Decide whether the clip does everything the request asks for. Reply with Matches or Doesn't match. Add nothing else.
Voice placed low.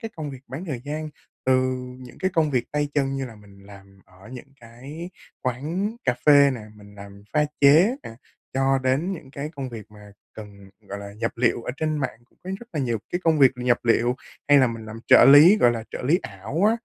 Matches